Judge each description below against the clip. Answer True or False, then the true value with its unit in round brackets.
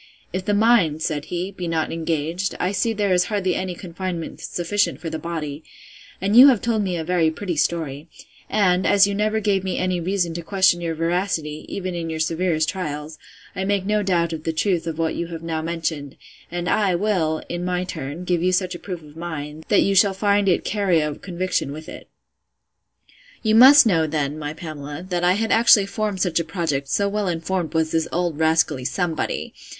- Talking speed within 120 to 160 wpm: False (205 wpm)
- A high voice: False (175 Hz)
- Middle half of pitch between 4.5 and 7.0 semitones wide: False (3.4 semitones)